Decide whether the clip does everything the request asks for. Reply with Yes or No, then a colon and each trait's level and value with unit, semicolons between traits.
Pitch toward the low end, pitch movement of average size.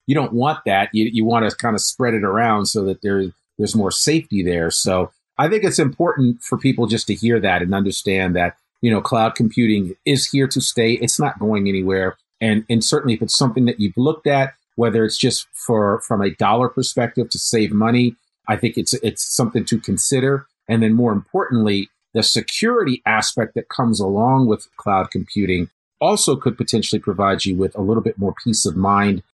Yes: low, 115 Hz; average, 3.8 semitones